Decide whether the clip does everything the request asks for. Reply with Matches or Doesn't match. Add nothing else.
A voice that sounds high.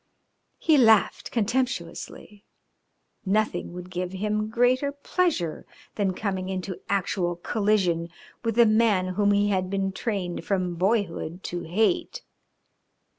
Matches